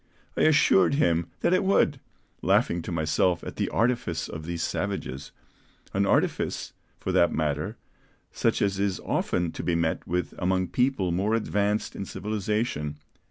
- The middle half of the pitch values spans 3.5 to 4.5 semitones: Yes, average, 4.2 semitones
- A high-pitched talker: No, very low, 90 Hz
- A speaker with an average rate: Yes, average, 155 wpm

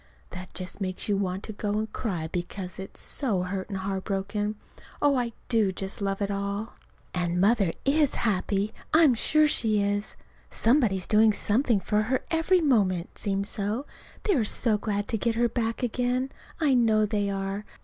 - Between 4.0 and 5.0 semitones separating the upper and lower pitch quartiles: No, average, 3.3 semitones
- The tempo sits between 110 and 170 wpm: No, average, 180 wpm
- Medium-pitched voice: No, high, 210 Hz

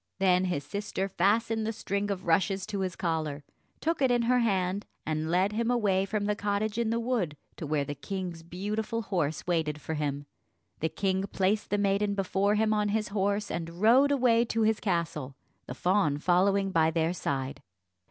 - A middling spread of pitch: Yes, average, 4.2 semitones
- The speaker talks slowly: No, average, 190 wpm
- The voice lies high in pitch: Yes, high, 195 Hz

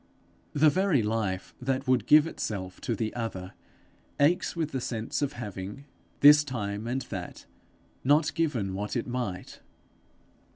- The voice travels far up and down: Yes, wide, 5.9 semitones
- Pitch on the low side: Yes, low, 120 Hz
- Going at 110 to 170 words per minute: Yes, average, 140 wpm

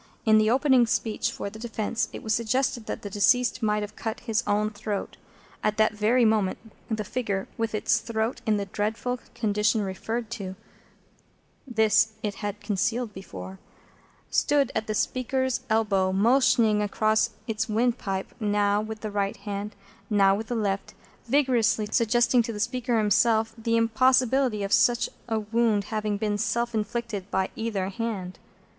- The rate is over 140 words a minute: Yes, average, 165 wpm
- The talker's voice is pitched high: Yes, high, 220 Hz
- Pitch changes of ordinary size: No, narrow, 2.1 semitones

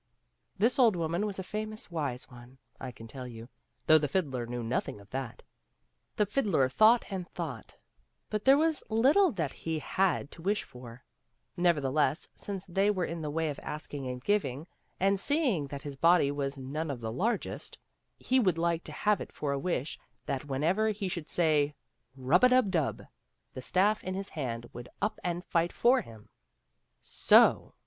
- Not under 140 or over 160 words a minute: No, average, 185 wpm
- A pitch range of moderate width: No, wide, 6.9 semitones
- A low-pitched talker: No, medium, 165 Hz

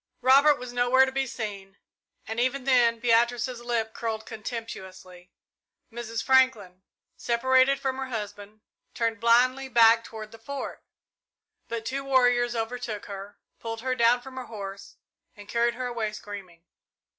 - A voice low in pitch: No, high, 235 Hz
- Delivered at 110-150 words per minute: Yes, average, 145 wpm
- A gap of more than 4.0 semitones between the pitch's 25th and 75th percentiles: No, average, 2.8 semitones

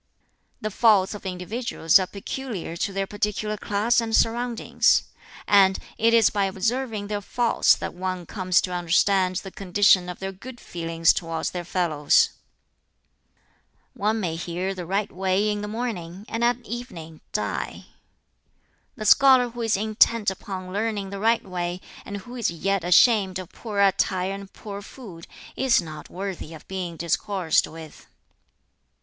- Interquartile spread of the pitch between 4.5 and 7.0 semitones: No, average, 3.4 semitones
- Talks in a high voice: Yes, high, 195 Hz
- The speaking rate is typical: Yes, average, 155 wpm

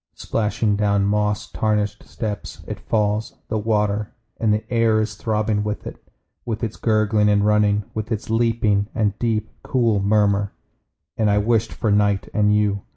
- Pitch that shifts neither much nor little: No, narrow, 1.1 semitones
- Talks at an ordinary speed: Yes, average, 160 wpm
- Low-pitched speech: Yes, low, 105 Hz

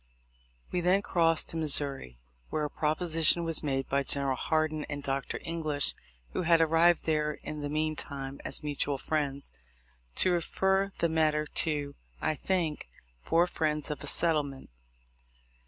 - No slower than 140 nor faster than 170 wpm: Yes, average, 150 wpm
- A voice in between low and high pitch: Yes, medium, 155 Hz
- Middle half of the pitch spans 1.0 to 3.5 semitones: Yes, narrow, 2.5 semitones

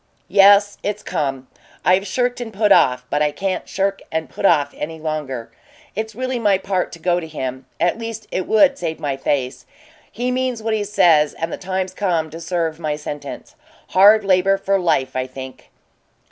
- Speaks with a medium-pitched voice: Yes, medium, 180 Hz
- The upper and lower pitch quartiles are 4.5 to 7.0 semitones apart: Yes, wide, 5.5 semitones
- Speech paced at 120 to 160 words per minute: No, average, 190 wpm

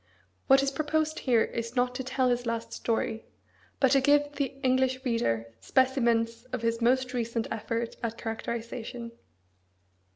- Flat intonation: Yes, narrow, 2.3 semitones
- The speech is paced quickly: No, average, 150 wpm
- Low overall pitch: No, high, 245 Hz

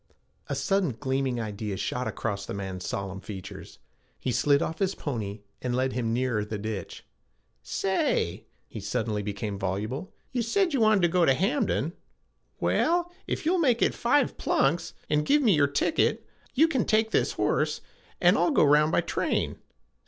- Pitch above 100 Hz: Yes, low, 135 Hz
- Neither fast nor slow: Yes, average, 170 wpm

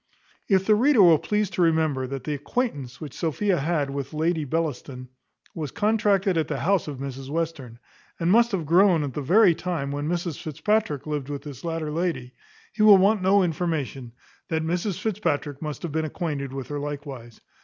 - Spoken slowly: No, average, 185 wpm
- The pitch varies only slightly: No, average, 4.4 semitones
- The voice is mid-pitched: Yes, medium, 160 Hz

